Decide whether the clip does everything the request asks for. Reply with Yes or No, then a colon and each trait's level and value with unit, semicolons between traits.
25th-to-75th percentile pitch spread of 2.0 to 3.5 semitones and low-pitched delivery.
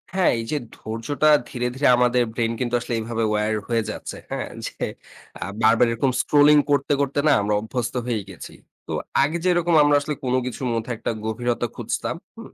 No: average, 3.9 semitones; low, 120 Hz